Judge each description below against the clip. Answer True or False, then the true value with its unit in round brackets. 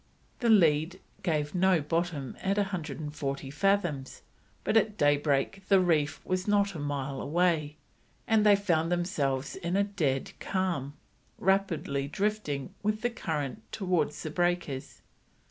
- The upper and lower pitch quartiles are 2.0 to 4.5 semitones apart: False (5.1 semitones)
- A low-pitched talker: False (170 Hz)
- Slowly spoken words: True (130 wpm)